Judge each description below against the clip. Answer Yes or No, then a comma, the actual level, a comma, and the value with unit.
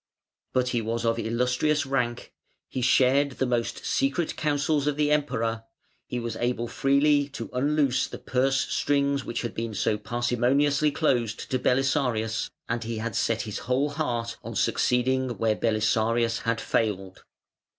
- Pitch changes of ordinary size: Yes, average, 3.3 semitones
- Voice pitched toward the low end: Yes, low, 125 Hz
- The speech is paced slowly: No, average, 150 wpm